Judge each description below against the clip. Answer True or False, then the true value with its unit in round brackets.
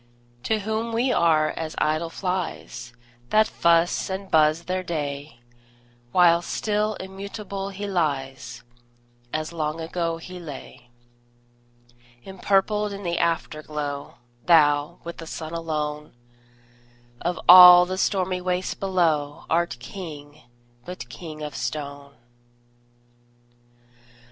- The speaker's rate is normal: False (110 wpm)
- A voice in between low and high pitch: True (170 Hz)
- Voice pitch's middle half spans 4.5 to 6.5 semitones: False (3.7 semitones)